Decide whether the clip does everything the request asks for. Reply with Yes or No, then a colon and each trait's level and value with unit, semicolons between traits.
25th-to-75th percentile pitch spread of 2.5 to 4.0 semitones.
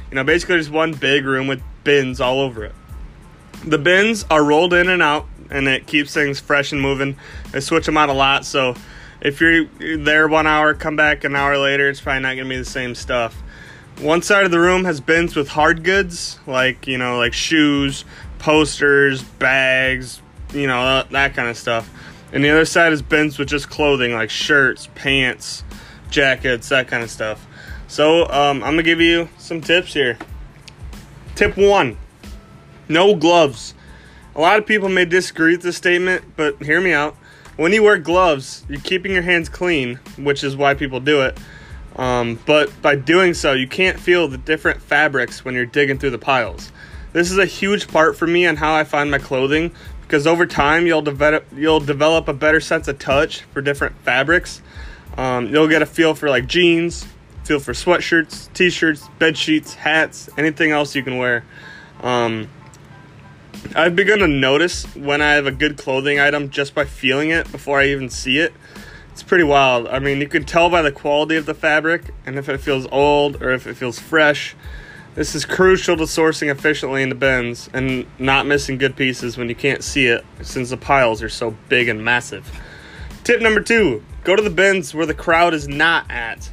Yes: average, 3.4 semitones